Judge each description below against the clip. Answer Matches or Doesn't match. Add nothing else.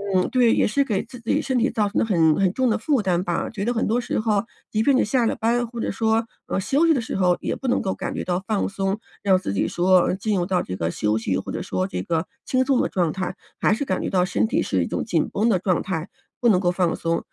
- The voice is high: Matches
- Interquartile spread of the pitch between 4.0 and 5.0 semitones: Matches